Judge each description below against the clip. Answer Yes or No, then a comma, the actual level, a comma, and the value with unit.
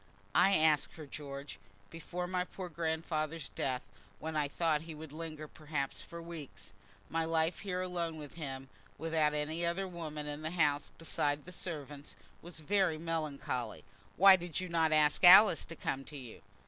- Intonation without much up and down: Yes, narrow, 2.3 semitones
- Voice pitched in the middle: Yes, medium, 160 Hz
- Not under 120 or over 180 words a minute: Yes, average, 175 wpm